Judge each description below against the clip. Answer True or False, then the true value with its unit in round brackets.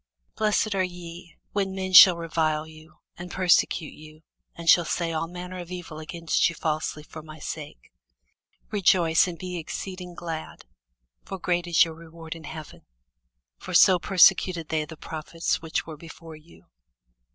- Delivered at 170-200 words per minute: False (160 wpm)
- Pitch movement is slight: True (2.1 semitones)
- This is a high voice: False (165 Hz)